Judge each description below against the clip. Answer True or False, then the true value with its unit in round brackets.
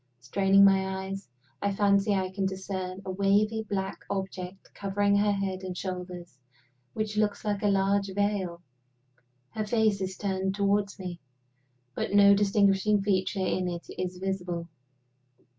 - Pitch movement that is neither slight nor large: False (1.3 semitones)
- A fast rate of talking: False (140 wpm)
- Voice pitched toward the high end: True (195 Hz)